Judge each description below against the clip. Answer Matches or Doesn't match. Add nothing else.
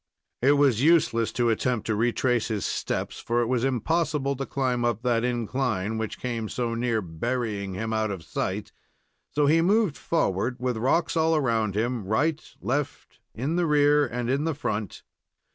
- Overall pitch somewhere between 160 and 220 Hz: Doesn't match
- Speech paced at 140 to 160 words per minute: Doesn't match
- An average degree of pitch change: Matches